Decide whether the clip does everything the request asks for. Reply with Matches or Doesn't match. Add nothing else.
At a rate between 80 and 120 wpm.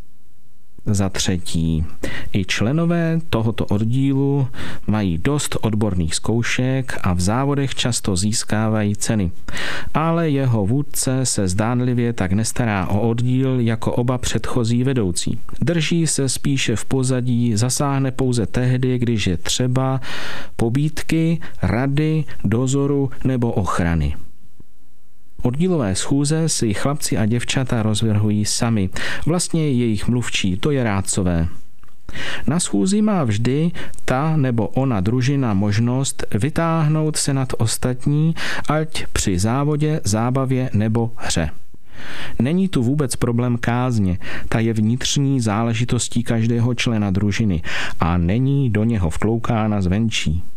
Matches